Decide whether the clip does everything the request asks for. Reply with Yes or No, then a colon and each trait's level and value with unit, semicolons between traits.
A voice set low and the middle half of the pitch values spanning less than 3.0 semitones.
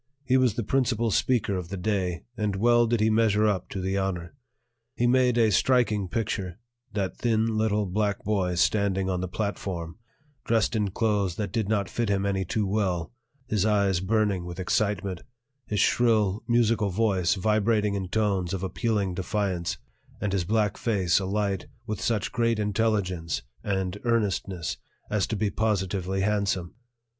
Yes: low, 100 Hz; narrow, 2.6 semitones